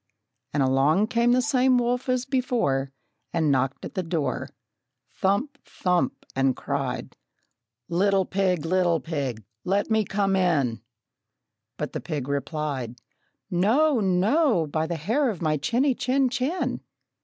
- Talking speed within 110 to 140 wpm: Yes, slow, 135 wpm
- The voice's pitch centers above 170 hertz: Yes, medium, 185 Hz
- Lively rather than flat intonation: Yes, wide, 8.3 semitones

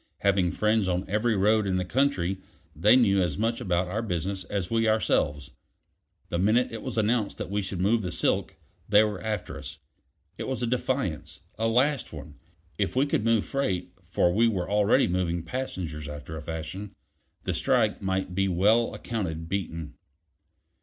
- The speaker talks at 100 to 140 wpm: No, average, 175 wpm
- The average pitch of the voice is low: Yes, low, 100 Hz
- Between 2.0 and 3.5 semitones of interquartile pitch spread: No, average, 4.2 semitones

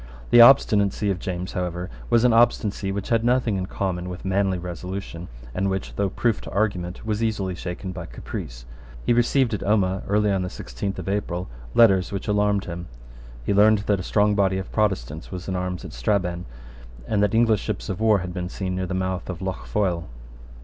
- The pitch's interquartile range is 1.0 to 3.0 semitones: Yes, narrow, 2.5 semitones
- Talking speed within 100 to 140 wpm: No, average, 200 wpm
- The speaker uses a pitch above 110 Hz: No, very low, 95 Hz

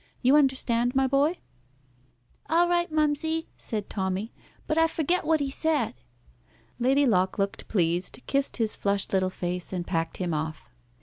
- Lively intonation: Yes, wide, 8.3 semitones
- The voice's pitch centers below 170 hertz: No, high, 245 Hz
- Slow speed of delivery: No, average, 150 wpm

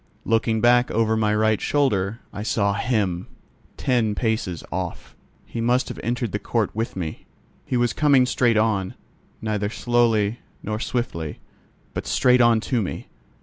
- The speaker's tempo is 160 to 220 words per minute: No, average, 150 wpm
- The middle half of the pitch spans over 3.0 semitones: No, narrow, 2.5 semitones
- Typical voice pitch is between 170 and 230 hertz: No, low, 110 Hz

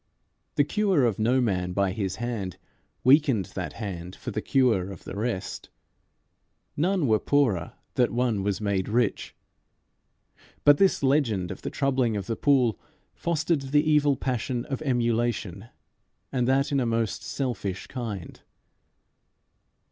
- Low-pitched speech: Yes, low, 120 Hz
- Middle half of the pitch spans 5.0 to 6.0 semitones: Yes, wide, 5.5 semitones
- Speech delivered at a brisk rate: No, average, 140 wpm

